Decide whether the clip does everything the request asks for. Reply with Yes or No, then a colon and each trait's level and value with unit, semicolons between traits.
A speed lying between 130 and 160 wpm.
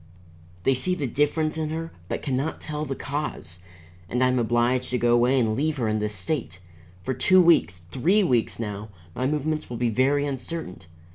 No: average, 200 wpm